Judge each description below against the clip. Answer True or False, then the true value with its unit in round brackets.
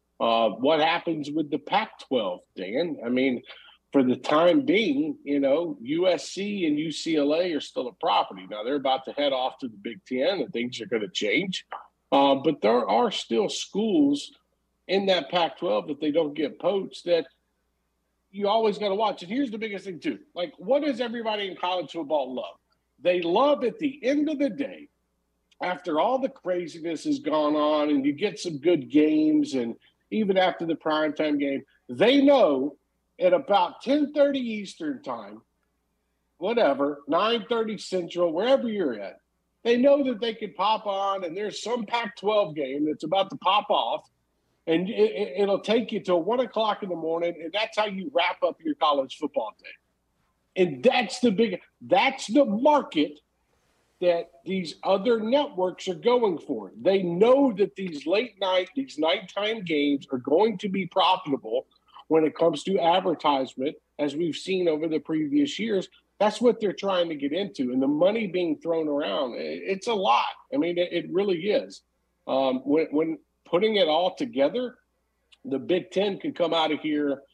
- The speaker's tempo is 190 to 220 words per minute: False (180 wpm)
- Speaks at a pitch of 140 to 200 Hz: True (185 Hz)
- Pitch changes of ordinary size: False (7.1 semitones)